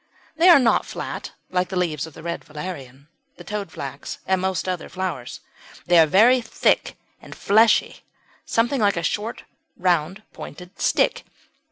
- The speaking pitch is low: No, medium, 185 Hz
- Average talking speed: Yes, average, 155 wpm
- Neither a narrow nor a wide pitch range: Yes, average, 4.6 semitones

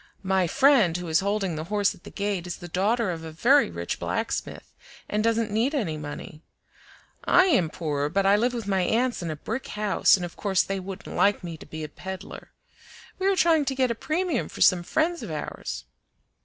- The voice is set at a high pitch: Yes, high, 195 Hz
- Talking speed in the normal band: No, fast, 215 wpm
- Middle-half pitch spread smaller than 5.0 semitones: No, wide, 5.4 semitones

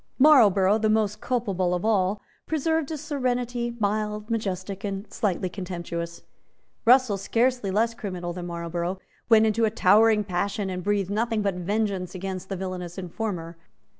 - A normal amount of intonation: Yes, average, 3.6 semitones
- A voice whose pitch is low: No, high, 205 Hz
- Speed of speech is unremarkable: Yes, average, 145 wpm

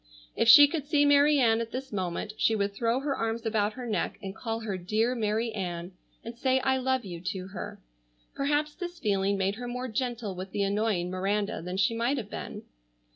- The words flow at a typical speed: No, fast, 210 wpm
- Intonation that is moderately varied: Yes, average, 4.6 semitones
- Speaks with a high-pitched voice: Yes, high, 225 Hz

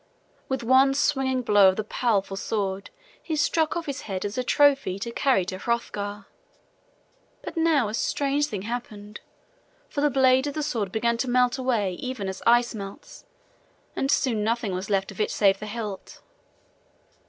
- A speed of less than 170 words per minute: No, average, 175 wpm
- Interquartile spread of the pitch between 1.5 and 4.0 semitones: No, average, 4.6 semitones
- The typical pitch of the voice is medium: No, high, 235 Hz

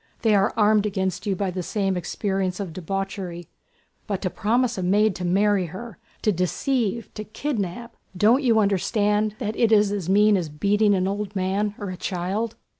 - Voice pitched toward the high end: Yes, high, 200 Hz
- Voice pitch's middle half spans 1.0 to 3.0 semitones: Yes, narrow, 2.4 semitones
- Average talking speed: Yes, average, 185 wpm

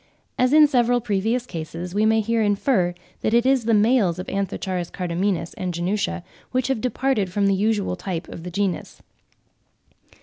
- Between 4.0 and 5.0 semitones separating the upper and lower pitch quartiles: Yes, average, 4.6 semitones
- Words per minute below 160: No, average, 170 wpm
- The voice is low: No, high, 205 Hz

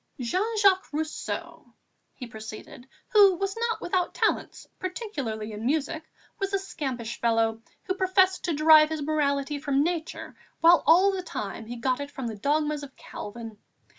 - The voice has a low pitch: No, very high, 300 Hz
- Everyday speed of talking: Yes, average, 160 wpm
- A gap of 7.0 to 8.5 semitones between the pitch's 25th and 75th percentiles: Yes, wide, 7.6 semitones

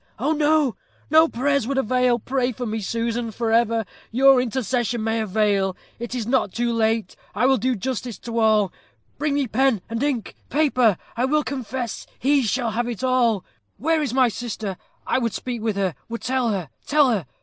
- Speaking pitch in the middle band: No, high, 240 Hz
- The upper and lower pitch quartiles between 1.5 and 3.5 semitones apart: Yes, average, 3.0 semitones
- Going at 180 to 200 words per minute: Yes, average, 185 wpm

